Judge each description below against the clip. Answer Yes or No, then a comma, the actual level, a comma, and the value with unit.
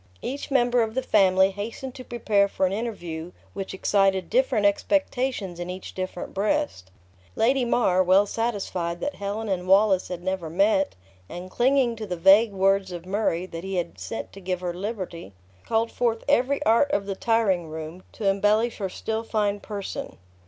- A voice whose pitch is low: No, high, 200 Hz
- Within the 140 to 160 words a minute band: No, average, 175 wpm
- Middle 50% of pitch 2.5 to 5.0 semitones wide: Yes, average, 3.7 semitones